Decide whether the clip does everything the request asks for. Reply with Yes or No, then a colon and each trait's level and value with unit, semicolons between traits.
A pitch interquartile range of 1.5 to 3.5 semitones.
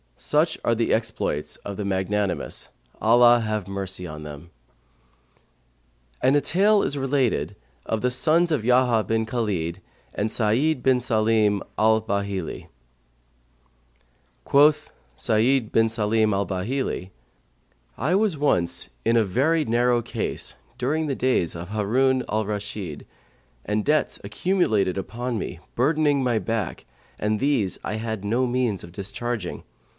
No: average, 4.2 semitones